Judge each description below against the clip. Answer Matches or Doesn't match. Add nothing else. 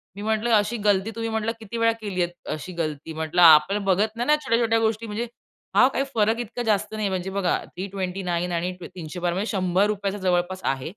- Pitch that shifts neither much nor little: Matches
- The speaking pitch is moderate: Doesn't match